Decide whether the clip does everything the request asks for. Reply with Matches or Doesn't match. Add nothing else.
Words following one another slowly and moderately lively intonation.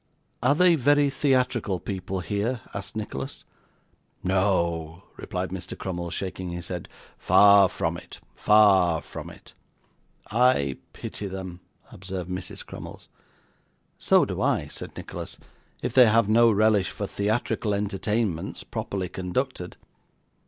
Matches